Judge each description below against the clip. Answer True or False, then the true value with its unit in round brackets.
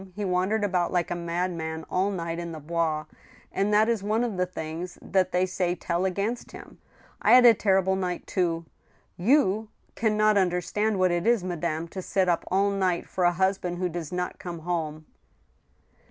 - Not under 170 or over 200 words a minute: True (195 wpm)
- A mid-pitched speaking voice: True (180 Hz)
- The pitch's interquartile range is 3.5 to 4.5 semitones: False (2.5 semitones)